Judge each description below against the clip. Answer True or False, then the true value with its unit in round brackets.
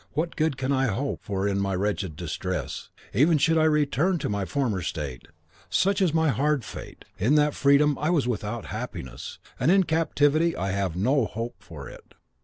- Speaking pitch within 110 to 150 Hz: True (135 Hz)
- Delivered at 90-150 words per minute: False (190 wpm)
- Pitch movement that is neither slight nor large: False (7.5 semitones)